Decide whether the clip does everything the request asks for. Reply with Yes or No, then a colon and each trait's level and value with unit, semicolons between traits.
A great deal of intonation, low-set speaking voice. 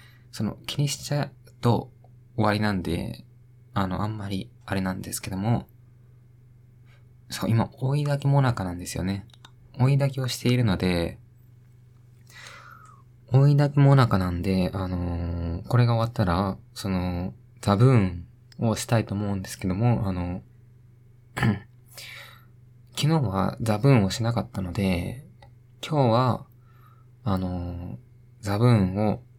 No: average, 3.8 semitones; low, 120 Hz